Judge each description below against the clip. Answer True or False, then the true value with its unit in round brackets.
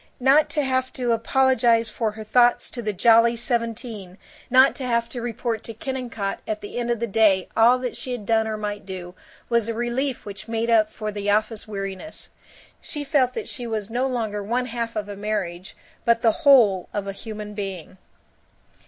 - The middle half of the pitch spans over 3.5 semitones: False (2.8 semitones)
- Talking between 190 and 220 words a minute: True (195 wpm)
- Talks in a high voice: True (230 Hz)